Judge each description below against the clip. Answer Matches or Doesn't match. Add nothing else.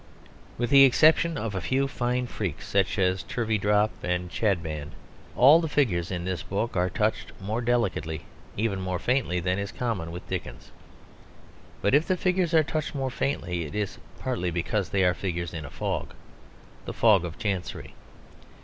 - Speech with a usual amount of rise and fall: Doesn't match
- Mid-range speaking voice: Doesn't match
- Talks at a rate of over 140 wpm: Matches